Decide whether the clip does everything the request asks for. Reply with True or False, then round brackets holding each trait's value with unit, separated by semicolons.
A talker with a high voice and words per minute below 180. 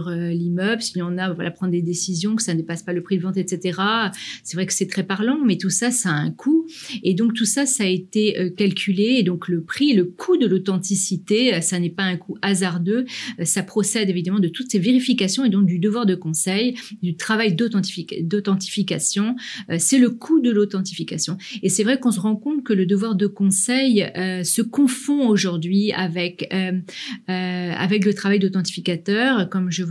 False (195 Hz; 205 wpm)